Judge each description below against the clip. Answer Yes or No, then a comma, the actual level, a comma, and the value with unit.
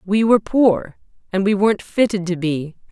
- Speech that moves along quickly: No, average, 185 wpm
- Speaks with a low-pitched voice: No, high, 200 Hz